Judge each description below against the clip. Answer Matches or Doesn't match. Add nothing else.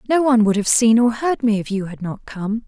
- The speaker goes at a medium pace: Doesn't match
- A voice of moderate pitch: Doesn't match